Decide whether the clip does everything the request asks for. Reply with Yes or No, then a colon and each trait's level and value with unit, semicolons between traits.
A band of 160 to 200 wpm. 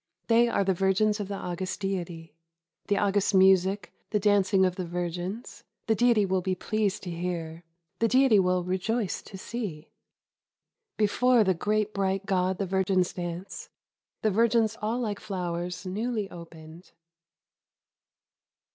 No: average, 150 wpm